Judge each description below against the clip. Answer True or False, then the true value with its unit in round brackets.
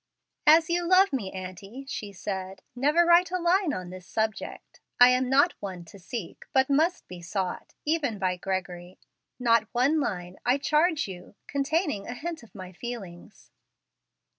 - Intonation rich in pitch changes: True (8.2 semitones)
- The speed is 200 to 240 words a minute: False (165 wpm)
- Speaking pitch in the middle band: False (240 Hz)